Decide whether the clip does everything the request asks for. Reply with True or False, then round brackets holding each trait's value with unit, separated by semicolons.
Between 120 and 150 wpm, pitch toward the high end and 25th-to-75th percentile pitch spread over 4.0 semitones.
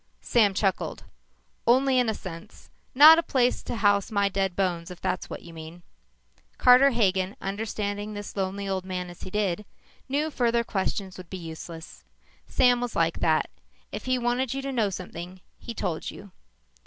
False (175 wpm; 200 Hz; 4.7 semitones)